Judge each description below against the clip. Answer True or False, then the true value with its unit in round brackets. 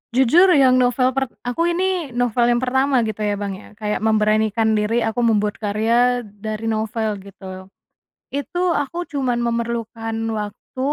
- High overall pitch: True (230 Hz)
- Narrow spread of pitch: False (3.1 semitones)